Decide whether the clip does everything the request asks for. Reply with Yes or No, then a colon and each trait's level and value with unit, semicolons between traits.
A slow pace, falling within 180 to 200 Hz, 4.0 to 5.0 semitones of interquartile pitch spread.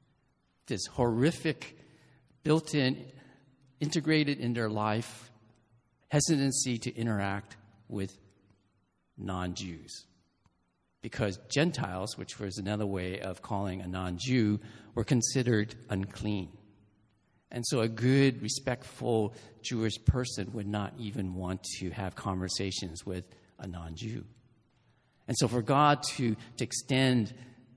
No: slow, 115 wpm; low, 110 Hz; average, 4.3 semitones